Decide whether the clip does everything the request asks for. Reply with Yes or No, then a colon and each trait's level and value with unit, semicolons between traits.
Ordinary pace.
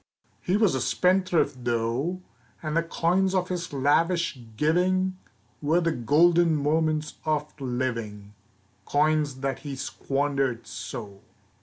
No: slow, 120 wpm